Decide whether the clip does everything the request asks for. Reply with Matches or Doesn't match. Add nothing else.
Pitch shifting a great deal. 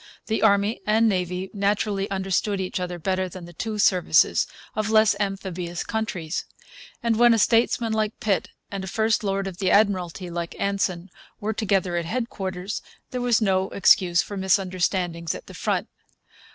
Doesn't match